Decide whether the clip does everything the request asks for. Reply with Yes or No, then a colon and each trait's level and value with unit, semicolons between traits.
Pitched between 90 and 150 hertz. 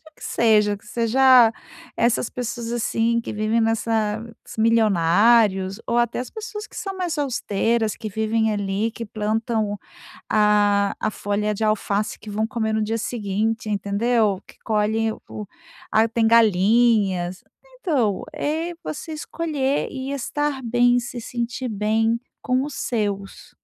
No: high, 225 Hz